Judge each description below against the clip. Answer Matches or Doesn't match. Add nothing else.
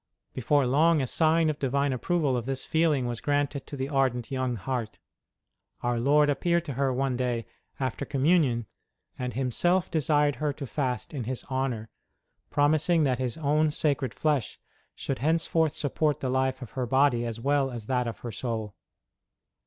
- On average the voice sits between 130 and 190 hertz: Matches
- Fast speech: Doesn't match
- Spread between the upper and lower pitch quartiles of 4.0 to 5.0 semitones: Doesn't match